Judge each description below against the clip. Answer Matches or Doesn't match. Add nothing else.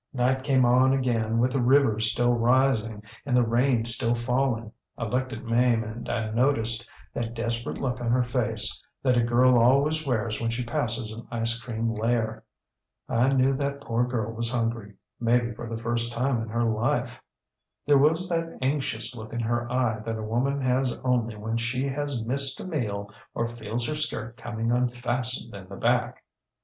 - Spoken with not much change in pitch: Matches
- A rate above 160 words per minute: Matches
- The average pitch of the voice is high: Doesn't match